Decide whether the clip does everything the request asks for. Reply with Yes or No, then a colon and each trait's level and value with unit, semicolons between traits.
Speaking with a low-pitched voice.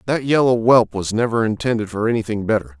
Yes: low, 115 Hz